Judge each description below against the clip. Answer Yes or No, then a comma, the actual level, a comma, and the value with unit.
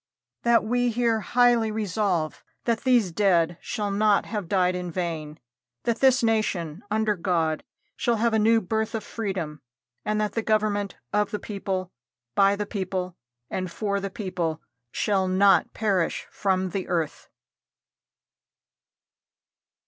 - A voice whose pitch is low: No, high, 200 Hz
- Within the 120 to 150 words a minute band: Yes, average, 140 wpm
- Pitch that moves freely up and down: No, average, 3.3 semitones